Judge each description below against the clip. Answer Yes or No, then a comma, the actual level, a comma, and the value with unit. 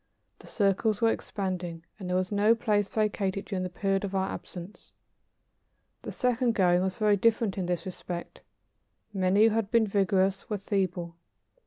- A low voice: No, high, 195 Hz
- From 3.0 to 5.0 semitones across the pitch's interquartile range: No, narrow, 2.4 semitones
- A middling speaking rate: Yes, average, 165 wpm